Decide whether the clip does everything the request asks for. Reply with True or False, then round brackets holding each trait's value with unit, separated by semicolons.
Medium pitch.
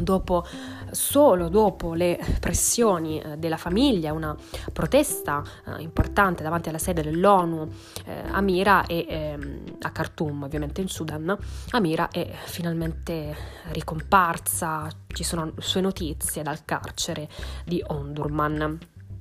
True (160 Hz)